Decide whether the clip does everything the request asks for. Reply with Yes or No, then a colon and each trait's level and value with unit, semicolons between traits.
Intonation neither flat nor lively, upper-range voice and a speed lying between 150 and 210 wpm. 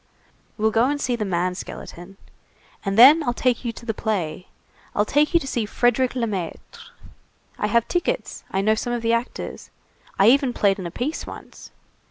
Yes: average, 4.1 semitones; high, 230 Hz; average, 190 wpm